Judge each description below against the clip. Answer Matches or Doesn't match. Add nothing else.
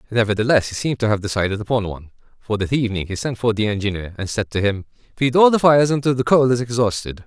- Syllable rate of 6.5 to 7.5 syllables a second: Matches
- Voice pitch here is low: Matches